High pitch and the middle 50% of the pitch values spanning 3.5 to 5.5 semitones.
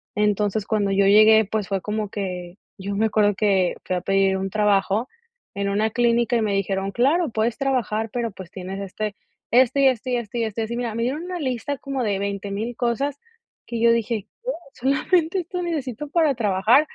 Yes: high, 220 Hz; average, 4.0 semitones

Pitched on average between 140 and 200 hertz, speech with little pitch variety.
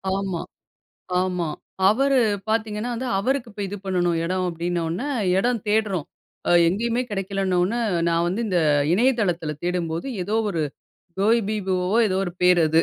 No: high, 190 Hz; average, 3.9 semitones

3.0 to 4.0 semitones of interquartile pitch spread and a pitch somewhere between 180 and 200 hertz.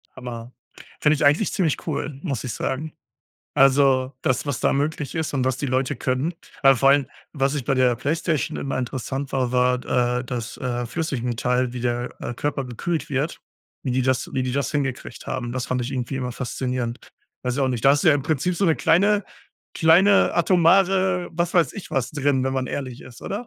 No: average, 3.6 semitones; low, 135 Hz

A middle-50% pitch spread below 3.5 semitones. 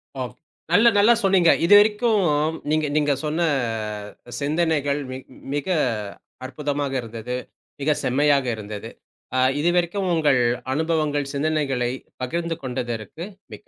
No: average, 4.6 semitones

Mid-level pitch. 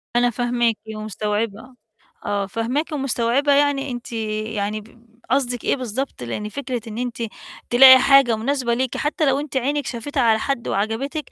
No: high, 240 Hz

